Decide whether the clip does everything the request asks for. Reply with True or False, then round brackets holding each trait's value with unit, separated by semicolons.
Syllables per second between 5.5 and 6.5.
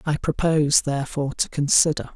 True (5.9 syllables/s)